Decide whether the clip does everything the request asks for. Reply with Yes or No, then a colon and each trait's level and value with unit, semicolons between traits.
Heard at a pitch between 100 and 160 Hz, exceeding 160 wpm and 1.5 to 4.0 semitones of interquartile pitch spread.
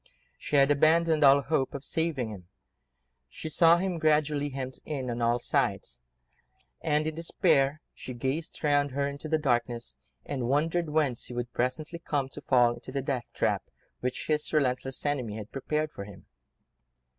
Yes: medium, 140 Hz; average, 170 wpm; average, 3.5 semitones